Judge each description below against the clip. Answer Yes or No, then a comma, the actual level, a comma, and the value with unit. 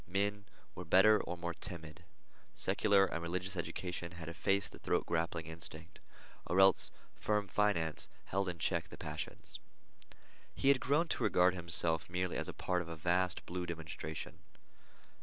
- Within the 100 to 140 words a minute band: No, average, 160 wpm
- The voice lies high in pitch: No, very low, 90 Hz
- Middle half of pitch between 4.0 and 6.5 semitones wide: No, narrow, 2.5 semitones